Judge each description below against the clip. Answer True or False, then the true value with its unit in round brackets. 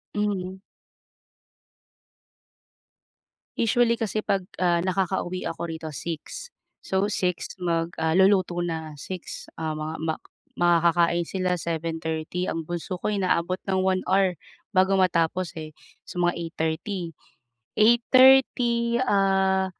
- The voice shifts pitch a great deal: False (2.8 semitones)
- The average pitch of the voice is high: False (180 Hz)